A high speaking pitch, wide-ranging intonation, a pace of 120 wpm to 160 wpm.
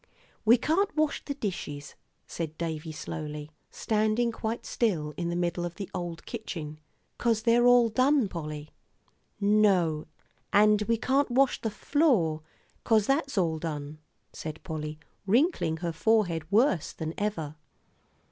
Yes: high, 195 Hz; wide, 6.5 semitones; average, 140 wpm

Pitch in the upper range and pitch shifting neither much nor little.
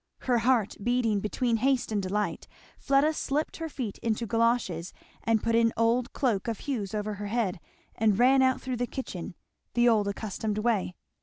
Yes: high, 230 Hz; average, 3.1 semitones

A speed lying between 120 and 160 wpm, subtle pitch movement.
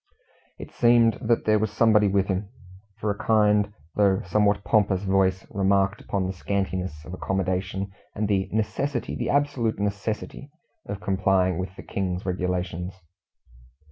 Yes: average, 140 wpm; narrow, 2.0 semitones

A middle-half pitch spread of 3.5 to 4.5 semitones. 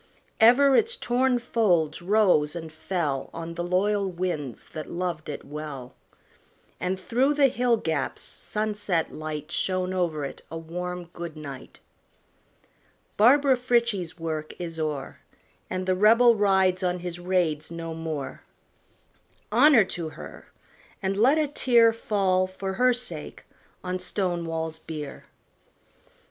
No: average, 5.2 semitones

